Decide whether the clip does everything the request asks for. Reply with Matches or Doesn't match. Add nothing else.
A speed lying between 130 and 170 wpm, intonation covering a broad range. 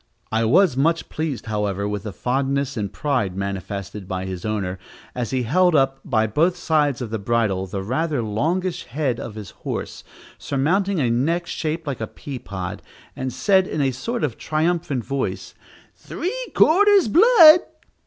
Matches